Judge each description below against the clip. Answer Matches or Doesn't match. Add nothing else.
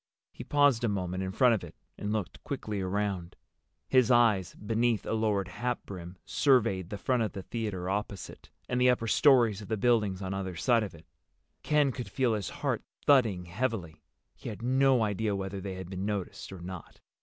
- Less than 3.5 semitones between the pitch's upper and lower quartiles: Doesn't match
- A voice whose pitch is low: Matches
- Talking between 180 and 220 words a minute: Matches